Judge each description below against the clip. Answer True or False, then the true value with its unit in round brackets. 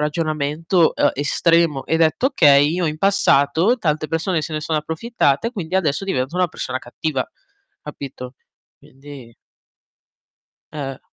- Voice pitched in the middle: True (155 Hz)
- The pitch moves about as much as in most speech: True (3.2 semitones)